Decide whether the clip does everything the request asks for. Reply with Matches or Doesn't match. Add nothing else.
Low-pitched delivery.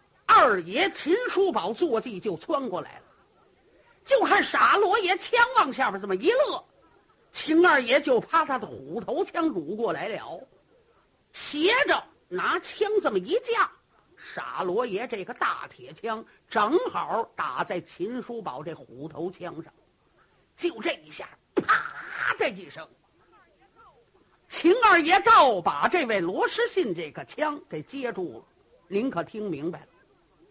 Doesn't match